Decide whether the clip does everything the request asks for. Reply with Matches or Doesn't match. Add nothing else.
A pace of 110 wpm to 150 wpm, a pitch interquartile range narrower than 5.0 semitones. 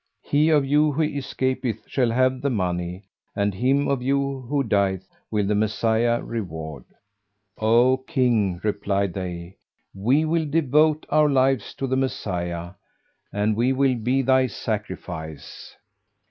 Doesn't match